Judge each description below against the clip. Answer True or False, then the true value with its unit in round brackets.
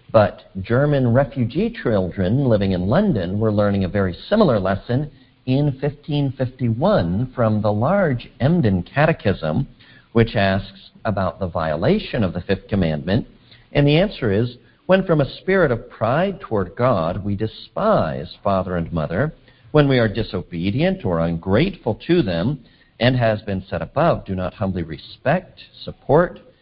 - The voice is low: True (115 Hz)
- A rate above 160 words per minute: False (145 wpm)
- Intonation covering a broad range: True (6.3 semitones)